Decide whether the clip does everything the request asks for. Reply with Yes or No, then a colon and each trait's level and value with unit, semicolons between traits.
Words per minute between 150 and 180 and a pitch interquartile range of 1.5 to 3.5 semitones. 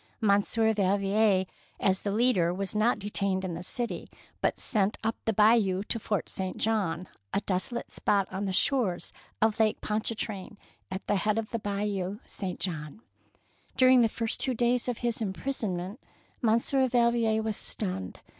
Yes: average, 160 wpm; average, 3.1 semitones